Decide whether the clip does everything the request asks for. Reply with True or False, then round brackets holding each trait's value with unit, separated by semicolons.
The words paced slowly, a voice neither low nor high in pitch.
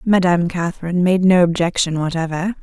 True (115 wpm; 175 Hz)